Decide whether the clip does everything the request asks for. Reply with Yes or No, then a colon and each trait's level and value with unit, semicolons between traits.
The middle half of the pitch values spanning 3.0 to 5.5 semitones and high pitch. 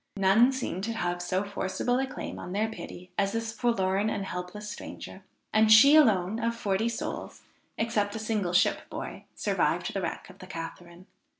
Yes: average, 3.4 semitones; high, 205 Hz